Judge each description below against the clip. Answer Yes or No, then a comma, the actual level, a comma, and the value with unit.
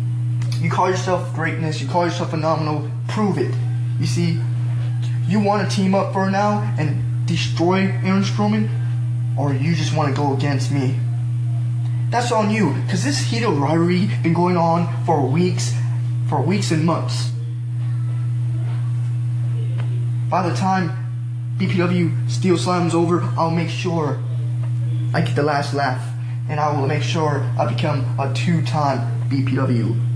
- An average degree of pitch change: No, narrow, 2.2 semitones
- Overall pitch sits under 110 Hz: No, low, 120 Hz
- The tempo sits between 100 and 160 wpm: Yes, average, 140 wpm